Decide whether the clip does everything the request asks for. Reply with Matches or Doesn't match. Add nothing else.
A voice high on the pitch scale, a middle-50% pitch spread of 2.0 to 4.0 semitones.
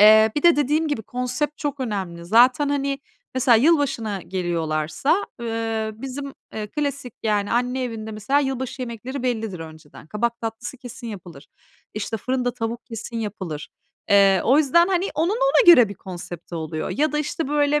Doesn't match